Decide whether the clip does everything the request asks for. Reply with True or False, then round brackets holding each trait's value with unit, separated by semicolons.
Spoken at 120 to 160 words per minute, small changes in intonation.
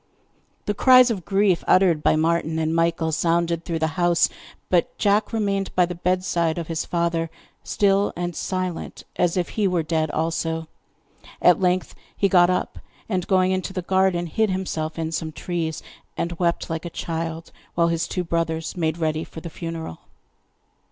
False (170 wpm; 2.2 semitones)